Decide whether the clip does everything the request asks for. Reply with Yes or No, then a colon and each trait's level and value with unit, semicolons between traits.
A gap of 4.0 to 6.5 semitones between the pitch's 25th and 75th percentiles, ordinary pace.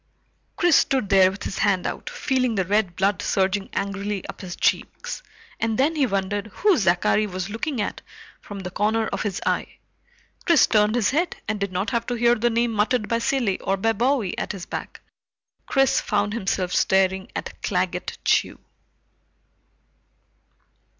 No: average, 3.6 semitones; average, 170 wpm